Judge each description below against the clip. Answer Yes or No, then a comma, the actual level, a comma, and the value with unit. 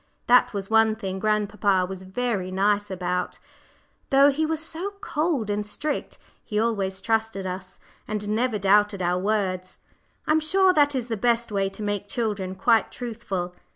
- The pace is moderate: Yes, average, 160 wpm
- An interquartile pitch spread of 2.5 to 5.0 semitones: Yes, average, 4.0 semitones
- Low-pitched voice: No, high, 210 Hz